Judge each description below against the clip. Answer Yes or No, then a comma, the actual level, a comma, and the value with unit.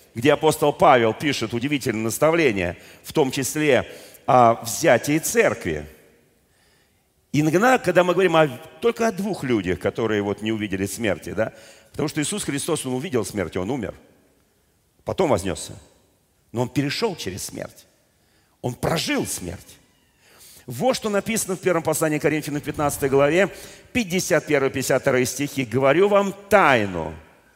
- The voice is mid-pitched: Yes, medium, 145 Hz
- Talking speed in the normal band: Yes, average, 135 wpm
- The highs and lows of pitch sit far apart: Yes, wide, 7.2 semitones